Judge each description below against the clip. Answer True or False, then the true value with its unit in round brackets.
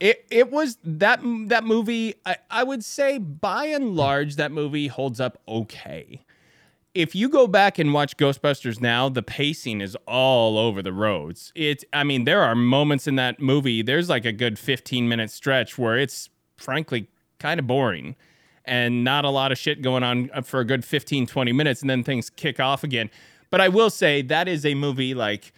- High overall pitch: False (140 Hz)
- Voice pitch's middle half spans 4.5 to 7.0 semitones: True (4.9 semitones)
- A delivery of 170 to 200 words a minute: True (195 wpm)